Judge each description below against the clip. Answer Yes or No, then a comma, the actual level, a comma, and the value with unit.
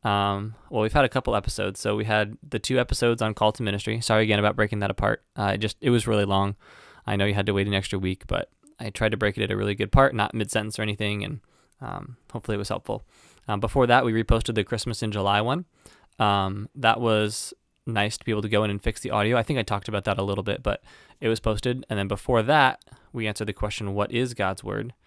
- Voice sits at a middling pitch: No, low, 105 Hz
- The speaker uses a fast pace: Yes, fast, 265 wpm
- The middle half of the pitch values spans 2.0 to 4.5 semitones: Yes, narrow, 2.5 semitones